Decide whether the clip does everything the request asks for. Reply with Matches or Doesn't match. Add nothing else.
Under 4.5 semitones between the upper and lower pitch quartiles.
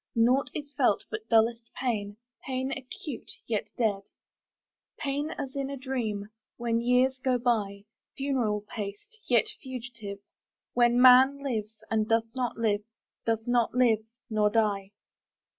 Matches